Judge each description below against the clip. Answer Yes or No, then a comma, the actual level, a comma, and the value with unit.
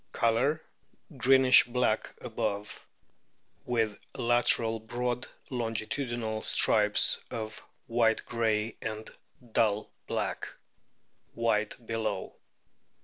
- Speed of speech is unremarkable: No, slow, 80 wpm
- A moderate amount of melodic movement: No, narrow, 1.8 semitones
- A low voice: Yes, low, 115 Hz